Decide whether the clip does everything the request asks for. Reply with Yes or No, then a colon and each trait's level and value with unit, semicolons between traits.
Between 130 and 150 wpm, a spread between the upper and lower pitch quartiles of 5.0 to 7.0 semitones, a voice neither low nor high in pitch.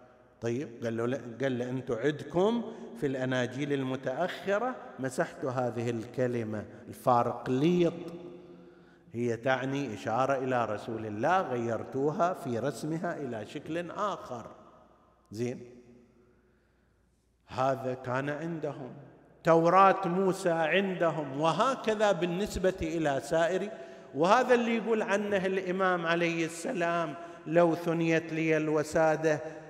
No: average, 90 wpm; wide, 5.5 semitones; medium, 155 Hz